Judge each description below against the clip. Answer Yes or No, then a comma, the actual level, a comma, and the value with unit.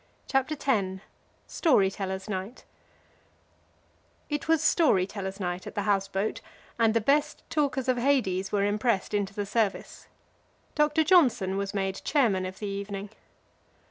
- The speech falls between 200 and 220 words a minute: No, average, 140 wpm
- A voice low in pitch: No, high, 205 Hz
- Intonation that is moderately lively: No, wide, 5.7 semitones